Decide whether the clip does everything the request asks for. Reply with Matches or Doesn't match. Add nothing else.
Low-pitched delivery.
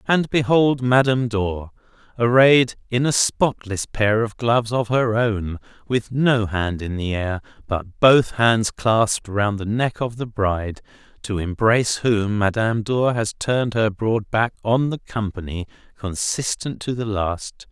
Matches